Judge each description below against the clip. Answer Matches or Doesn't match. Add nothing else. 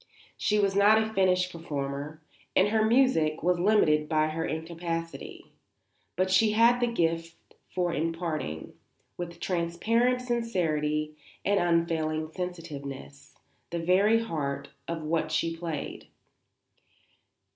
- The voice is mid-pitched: Matches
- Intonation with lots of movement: Doesn't match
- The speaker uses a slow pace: Matches